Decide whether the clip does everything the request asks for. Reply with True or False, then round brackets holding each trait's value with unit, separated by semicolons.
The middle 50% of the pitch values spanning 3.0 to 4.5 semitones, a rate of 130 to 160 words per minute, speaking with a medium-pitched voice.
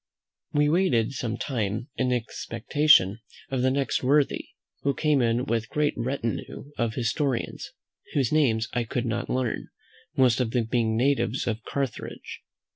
False (3.4 semitones; 150 wpm; 125 Hz)